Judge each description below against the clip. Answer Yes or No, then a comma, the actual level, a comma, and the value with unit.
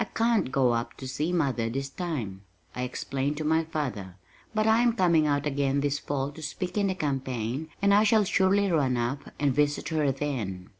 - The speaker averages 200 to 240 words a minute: Yes, fast, 205 wpm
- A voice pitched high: No, medium, 145 Hz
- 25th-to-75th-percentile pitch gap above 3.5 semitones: Yes, average, 4.9 semitones